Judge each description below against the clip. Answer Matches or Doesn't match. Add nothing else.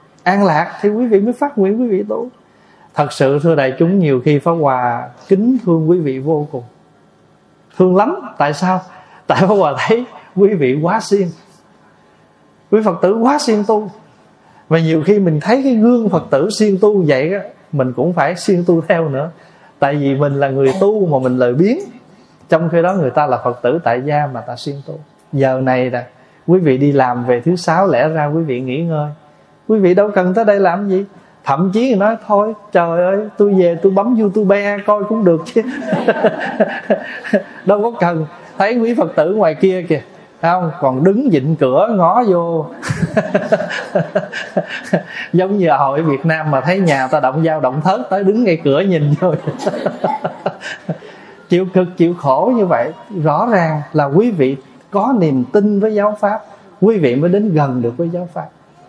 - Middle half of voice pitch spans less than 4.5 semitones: Doesn't match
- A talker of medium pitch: Matches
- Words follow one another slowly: Doesn't match